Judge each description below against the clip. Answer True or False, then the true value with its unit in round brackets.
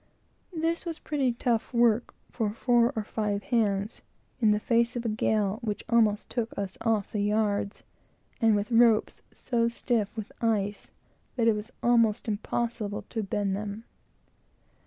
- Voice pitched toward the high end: True (220 Hz)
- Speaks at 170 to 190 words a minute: False (155 wpm)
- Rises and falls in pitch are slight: True (2.3 semitones)